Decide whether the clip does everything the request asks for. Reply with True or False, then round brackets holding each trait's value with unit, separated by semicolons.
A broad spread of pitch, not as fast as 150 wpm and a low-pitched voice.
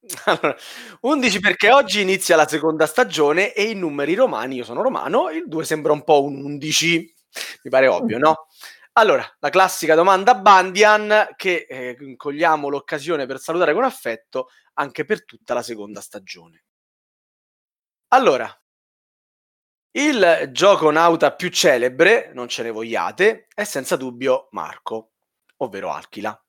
False (6.0 semitones; 140 wpm; 165 Hz)